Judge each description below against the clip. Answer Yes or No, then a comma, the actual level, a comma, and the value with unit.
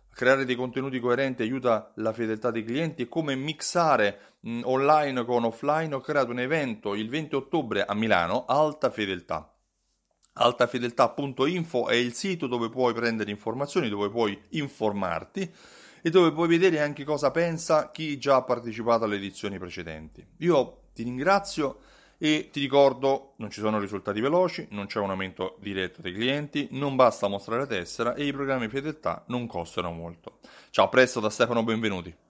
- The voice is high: No, low, 125 Hz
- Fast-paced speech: No, average, 160 wpm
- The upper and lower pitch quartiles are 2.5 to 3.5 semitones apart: No, average, 5.1 semitones